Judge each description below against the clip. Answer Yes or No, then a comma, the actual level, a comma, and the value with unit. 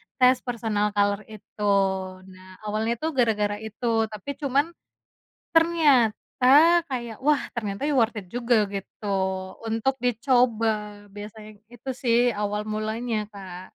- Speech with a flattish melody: No, average, 3.2 semitones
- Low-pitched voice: No, high, 220 Hz